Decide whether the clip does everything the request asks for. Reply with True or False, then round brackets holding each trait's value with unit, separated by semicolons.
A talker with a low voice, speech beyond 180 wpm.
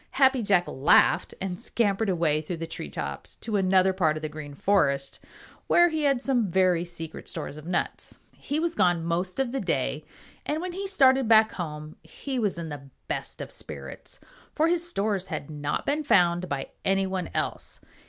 False (185 Hz; 190 wpm)